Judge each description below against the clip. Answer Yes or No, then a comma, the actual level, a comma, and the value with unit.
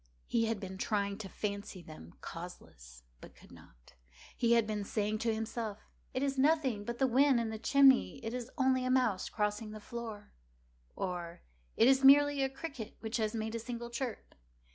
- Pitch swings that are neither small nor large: Yes, average, 3.8 semitones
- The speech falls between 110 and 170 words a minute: No, average, 180 wpm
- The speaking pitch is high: Yes, high, 225 Hz